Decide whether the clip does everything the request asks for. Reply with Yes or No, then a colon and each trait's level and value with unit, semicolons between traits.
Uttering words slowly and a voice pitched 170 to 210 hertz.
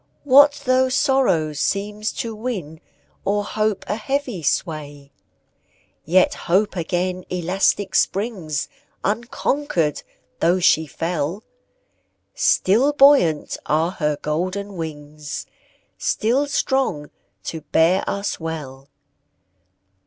Yes: slow, 95 wpm; medium, 185 Hz